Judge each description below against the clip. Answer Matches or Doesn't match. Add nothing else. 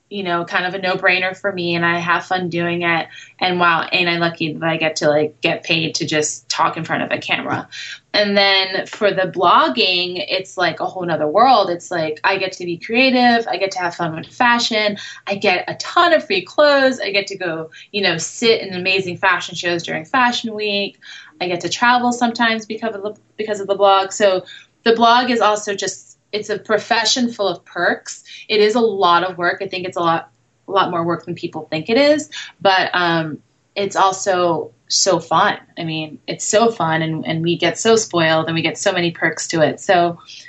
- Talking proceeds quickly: Matches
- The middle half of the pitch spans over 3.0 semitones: Matches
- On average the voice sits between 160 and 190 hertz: Matches